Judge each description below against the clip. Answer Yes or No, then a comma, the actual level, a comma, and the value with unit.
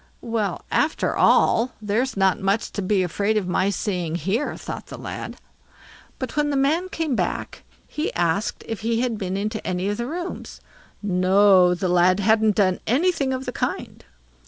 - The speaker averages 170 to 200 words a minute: Yes, average, 175 wpm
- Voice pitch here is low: No, high, 210 Hz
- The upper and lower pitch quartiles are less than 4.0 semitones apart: No, average, 5.0 semitones